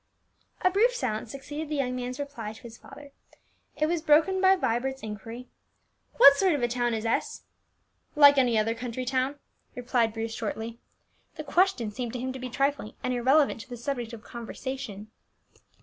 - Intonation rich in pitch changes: No, average, 3.7 semitones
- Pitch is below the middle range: No, very high, 255 Hz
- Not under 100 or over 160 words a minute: No, average, 180 wpm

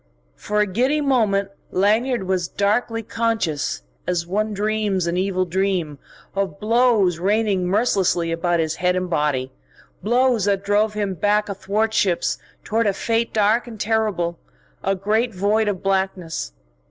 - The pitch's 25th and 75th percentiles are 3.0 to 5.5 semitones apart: Yes, average, 3.3 semitones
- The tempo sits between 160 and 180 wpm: No, average, 140 wpm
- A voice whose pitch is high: Yes, high, 200 Hz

